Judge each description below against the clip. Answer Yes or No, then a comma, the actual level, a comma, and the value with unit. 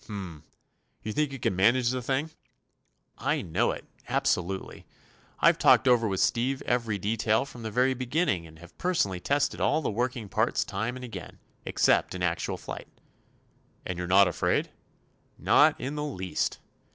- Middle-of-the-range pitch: No, low, 115 Hz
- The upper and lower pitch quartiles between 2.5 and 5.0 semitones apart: No, wide, 5.4 semitones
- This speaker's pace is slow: No, average, 165 wpm